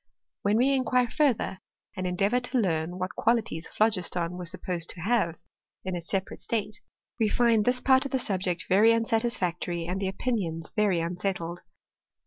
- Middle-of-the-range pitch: No, high, 195 Hz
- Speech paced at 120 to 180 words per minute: Yes, average, 160 wpm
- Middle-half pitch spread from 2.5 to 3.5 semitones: No, average, 4.7 semitones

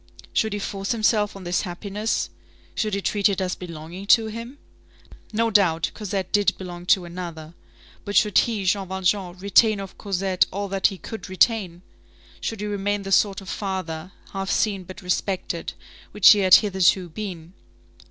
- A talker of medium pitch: No, high, 195 Hz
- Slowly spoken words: No, average, 170 wpm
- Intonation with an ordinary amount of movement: No, narrow, 2.3 semitones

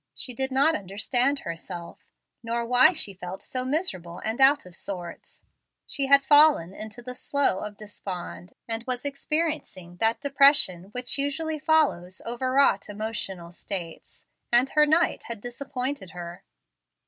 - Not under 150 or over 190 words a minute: No, average, 140 wpm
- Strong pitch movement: Yes, wide, 6.6 semitones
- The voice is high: Yes, high, 240 Hz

